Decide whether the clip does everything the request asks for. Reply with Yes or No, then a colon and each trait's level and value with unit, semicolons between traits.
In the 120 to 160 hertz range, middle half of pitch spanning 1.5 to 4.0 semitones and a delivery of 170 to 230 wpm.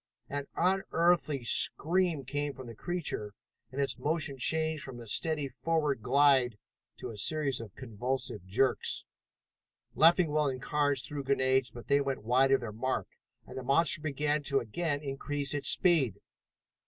No: medium, 140 Hz; average, 3.1 semitones; average, 155 wpm